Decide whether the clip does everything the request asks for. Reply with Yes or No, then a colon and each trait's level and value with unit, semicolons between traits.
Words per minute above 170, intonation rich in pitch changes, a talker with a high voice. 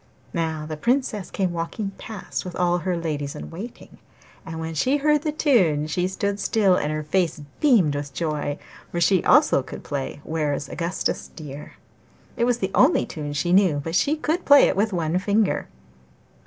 No: average, 185 wpm; wide, 5.7 semitones; medium, 175 Hz